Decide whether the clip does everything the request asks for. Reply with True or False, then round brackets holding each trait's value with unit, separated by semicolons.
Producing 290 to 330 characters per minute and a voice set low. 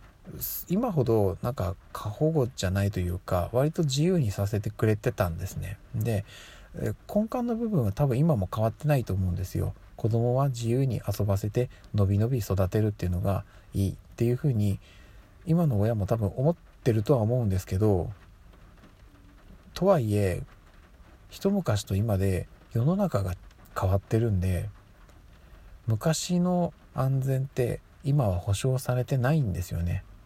True (295 characters per minute; 105 Hz)